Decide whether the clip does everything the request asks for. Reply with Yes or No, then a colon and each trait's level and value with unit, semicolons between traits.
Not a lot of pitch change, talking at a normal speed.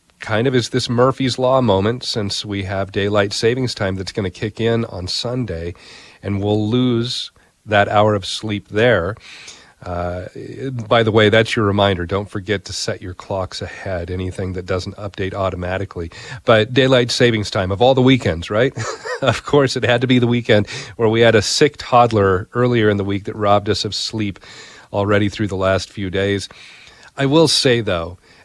No: average, 3.8 semitones; average, 190 wpm